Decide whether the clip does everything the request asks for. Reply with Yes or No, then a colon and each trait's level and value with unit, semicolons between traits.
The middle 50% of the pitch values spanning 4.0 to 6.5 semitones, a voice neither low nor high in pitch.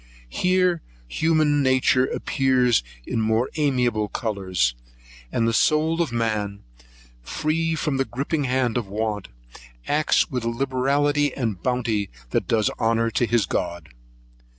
No: average, 4.8 semitones; low, 125 Hz